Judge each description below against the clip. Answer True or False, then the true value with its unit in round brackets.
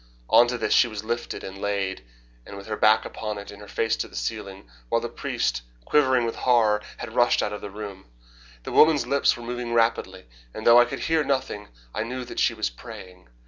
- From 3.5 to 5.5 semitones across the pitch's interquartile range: False (3.1 semitones)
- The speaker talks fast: True (220 wpm)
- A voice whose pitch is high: False (110 Hz)